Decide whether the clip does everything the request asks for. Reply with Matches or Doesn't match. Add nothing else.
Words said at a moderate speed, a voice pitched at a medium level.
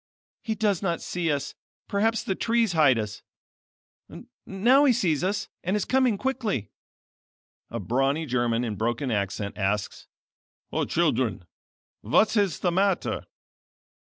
Doesn't match